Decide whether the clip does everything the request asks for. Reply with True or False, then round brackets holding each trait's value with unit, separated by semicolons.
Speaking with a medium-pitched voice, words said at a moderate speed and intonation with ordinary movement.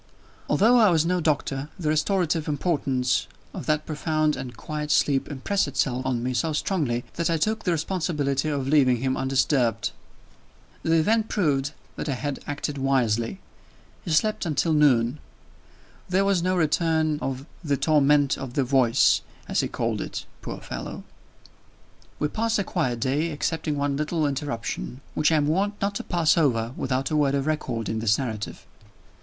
True (150 Hz; 170 wpm; 3.6 semitones)